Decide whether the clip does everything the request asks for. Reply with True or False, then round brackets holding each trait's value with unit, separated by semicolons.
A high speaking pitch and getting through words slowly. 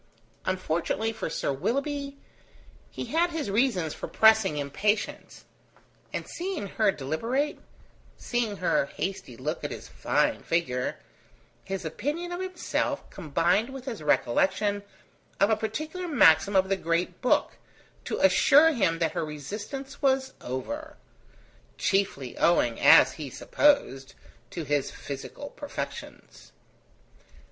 True (200 Hz; 120 wpm)